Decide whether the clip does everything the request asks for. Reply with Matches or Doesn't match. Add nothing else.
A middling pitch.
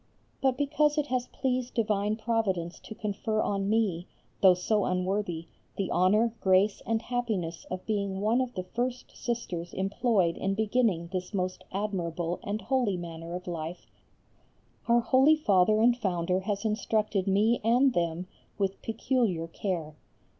Doesn't match